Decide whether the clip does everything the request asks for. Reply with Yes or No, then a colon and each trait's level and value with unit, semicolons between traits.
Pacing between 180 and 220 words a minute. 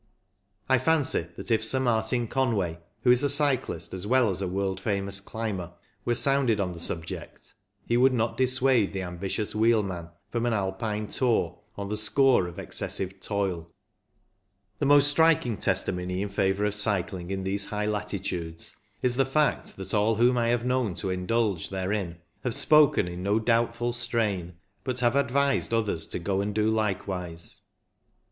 No: average, 165 wpm